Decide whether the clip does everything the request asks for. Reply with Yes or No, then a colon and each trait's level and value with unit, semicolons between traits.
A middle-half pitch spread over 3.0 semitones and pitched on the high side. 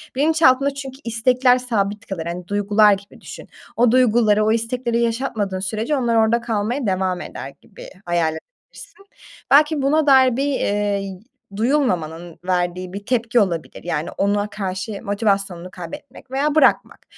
Yes: average, 5.0 semitones; high, 215 Hz